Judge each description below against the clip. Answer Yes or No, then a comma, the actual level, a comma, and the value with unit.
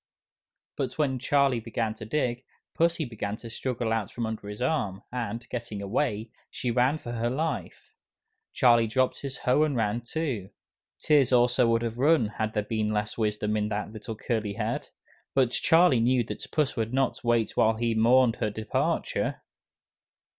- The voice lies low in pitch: Yes, low, 115 Hz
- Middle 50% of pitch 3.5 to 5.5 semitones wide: No, average, 2.9 semitones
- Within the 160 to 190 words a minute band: Yes, average, 170 wpm